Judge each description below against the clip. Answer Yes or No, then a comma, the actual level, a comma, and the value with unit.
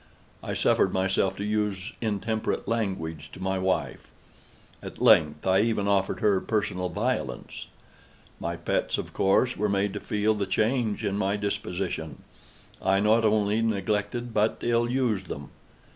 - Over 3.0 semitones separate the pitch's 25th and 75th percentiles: No, narrow, 2.5 semitones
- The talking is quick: No, average, 145 wpm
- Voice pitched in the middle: No, low, 100 Hz